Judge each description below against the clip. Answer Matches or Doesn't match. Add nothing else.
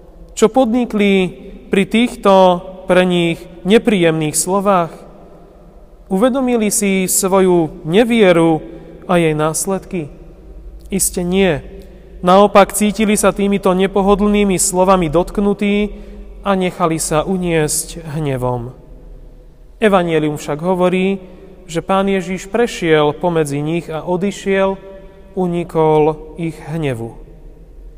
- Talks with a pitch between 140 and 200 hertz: Matches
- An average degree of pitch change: Matches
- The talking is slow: Matches